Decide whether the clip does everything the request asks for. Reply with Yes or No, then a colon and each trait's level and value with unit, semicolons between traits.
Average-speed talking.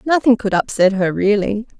Yes: average, 170 wpm